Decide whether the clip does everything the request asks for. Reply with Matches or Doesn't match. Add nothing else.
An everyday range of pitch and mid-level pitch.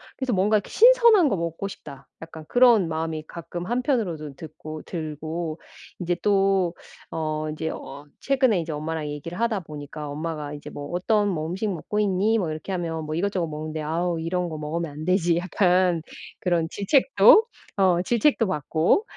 Matches